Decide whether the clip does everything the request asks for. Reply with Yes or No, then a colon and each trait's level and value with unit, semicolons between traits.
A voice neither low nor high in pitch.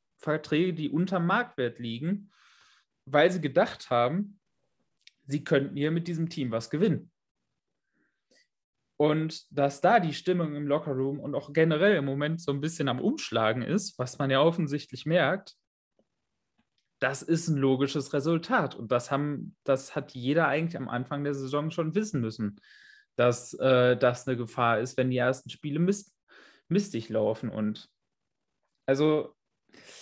Yes: medium, 145 Hz